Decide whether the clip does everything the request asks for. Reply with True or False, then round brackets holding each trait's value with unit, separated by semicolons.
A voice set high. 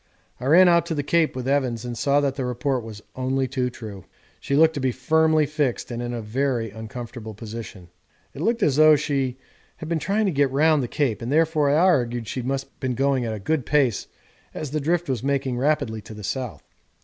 False (135 Hz)